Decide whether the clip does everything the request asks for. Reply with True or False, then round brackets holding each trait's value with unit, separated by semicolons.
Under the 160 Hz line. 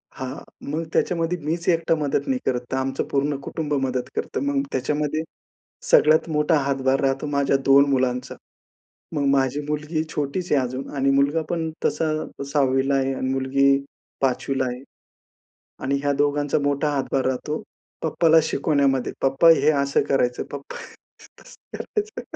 True (140 Hz)